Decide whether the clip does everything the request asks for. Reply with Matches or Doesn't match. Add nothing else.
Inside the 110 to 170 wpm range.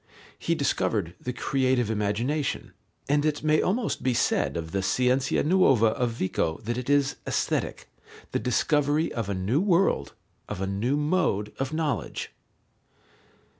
Matches